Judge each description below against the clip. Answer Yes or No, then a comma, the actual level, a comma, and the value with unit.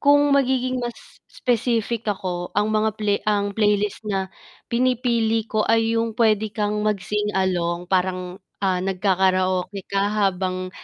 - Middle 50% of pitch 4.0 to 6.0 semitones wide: No, average, 3.2 semitones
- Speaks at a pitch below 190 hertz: No, high, 210 Hz